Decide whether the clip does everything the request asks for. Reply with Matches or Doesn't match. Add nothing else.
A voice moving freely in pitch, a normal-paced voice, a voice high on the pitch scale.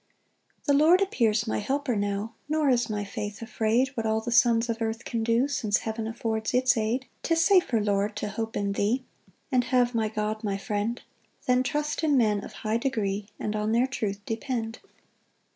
Doesn't match